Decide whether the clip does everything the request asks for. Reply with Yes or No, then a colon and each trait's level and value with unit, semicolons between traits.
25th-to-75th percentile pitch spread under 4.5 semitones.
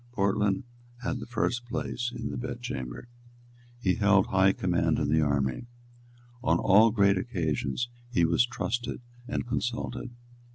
No: wide, 5.5 semitones